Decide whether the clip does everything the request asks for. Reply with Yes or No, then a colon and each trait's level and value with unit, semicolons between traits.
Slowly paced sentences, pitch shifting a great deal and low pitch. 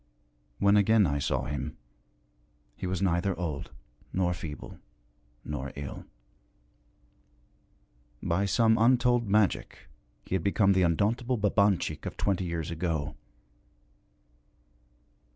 No: slow, 105 wpm; average, 4.8 semitones; very low, 90 Hz